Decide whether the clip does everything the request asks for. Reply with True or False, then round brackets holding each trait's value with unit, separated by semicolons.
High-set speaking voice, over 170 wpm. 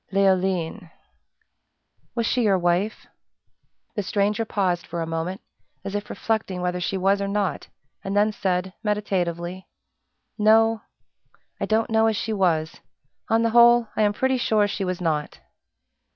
False (200 Hz; 150 wpm)